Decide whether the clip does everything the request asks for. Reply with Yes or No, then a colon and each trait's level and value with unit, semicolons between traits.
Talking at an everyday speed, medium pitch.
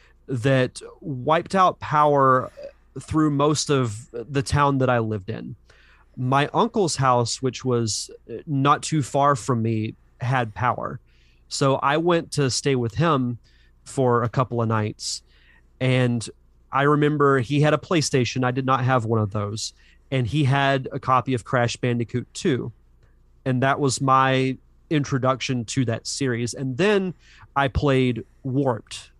No: average, 150 wpm; low, 130 Hz